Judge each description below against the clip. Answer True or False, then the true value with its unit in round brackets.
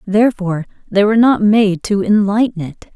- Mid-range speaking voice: False (205 Hz)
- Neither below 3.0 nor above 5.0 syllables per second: False (5.4 syllables/s)